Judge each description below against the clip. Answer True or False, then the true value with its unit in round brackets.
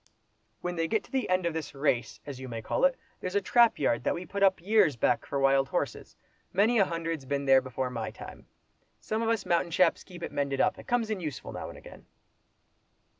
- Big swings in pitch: True (6.5 semitones)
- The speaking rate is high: True (225 wpm)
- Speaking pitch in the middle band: True (170 Hz)